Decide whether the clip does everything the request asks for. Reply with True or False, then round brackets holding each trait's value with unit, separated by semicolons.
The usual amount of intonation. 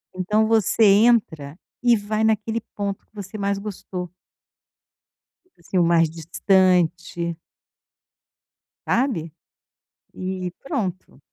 True (3.8 semitones)